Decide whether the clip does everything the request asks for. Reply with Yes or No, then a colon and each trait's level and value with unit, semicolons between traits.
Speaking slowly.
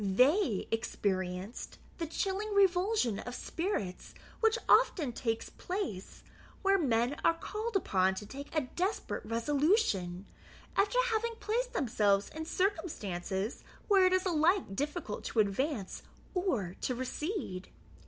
Yes: slow, 125 wpm